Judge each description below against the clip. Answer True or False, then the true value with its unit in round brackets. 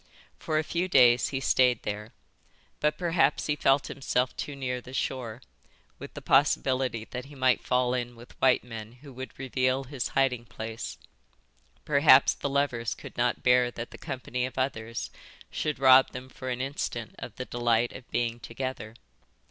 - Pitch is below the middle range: True (130 Hz)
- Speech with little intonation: True (2.1 semitones)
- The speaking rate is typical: True (170 wpm)